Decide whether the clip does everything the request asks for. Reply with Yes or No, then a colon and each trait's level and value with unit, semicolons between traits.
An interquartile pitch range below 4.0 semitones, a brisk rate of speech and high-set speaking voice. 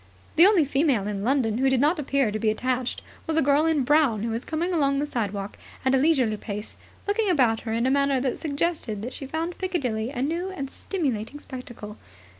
No: wide, 5.4 semitones; fast, 215 wpm; very high, 270 Hz